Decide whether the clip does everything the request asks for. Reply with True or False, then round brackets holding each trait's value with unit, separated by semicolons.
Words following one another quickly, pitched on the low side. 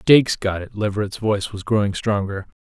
False (185 wpm; 105 Hz)